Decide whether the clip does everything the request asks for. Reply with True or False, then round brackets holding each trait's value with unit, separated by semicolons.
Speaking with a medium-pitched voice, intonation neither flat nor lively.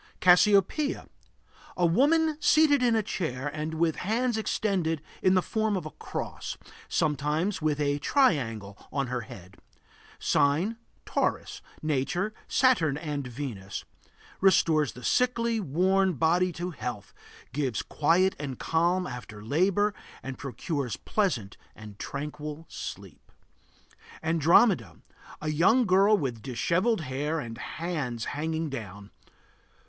False (160 Hz; 6.0 semitones)